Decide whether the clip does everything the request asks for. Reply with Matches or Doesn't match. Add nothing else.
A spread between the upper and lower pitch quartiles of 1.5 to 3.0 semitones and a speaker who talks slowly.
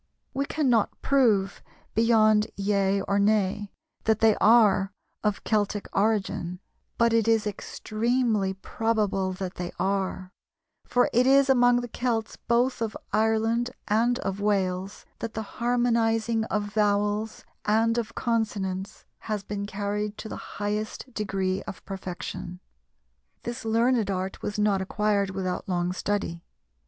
Matches